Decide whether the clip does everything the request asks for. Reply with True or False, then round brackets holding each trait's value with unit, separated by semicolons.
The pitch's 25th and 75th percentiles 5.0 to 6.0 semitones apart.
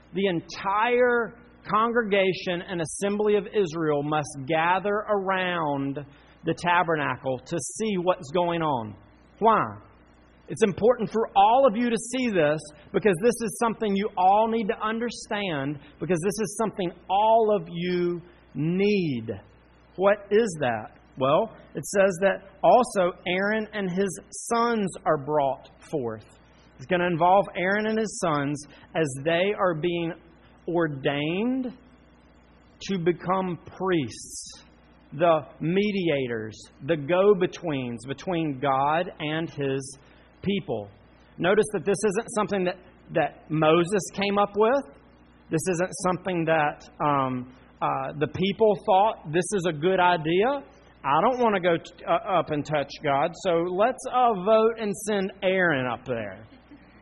True (5.5 semitones)